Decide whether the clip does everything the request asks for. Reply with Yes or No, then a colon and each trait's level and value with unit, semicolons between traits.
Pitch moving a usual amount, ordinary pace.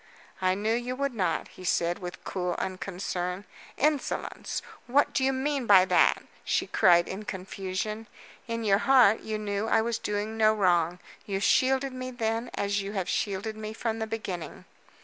Yes: average, 3.5 semitones; average, 170 wpm